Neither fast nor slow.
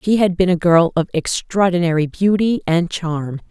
Yes: average, 170 wpm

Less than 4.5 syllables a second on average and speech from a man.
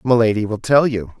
No: 5.7 syllables/s; male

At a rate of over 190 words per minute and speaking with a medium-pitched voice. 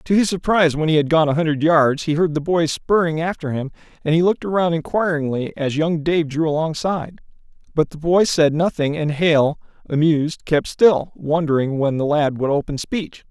Yes: average, 200 wpm; medium, 160 Hz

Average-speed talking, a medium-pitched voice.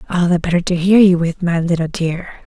No: fast, 235 wpm; medium, 175 Hz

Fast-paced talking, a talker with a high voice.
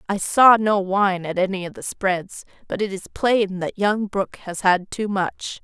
Yes: fast, 215 wpm; high, 195 Hz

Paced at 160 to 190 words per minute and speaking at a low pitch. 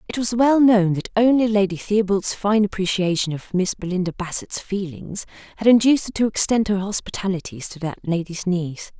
No: average, 175 wpm; high, 195 Hz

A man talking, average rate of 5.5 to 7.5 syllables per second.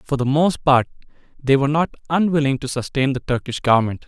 Yes: male; 5.9 syllables/s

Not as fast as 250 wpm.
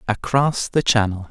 Yes: average, 140 wpm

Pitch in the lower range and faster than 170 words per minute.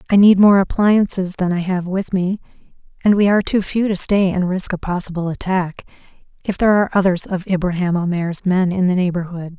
No: medium, 185 Hz; average, 200 wpm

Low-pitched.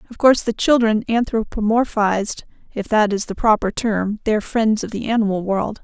No: high, 215 Hz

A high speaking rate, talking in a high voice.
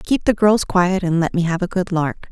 No: fast, 285 wpm; medium, 180 Hz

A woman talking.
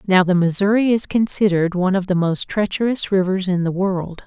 Yes: female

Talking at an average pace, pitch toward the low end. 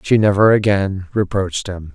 Yes: average, 155 wpm; low, 100 Hz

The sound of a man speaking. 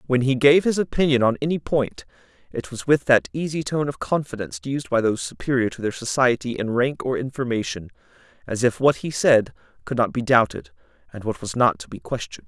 Yes: male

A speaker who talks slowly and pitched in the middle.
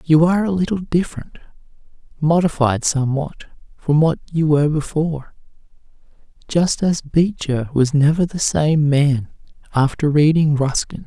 Yes: slow, 115 wpm; medium, 155 Hz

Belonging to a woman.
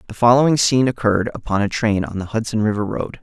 No: male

